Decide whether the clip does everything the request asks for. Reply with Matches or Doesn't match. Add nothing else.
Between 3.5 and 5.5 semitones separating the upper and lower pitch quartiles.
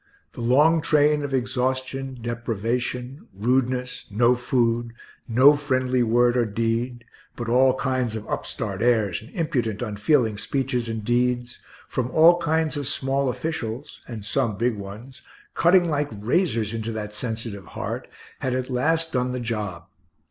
Doesn't match